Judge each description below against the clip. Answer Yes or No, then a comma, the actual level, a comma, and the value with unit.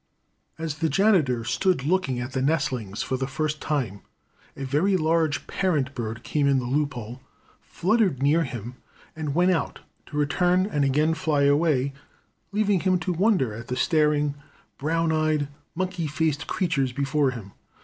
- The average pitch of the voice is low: No, medium, 150 Hz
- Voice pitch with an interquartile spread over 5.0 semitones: No, average, 3.9 semitones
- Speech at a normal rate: Yes, average, 160 wpm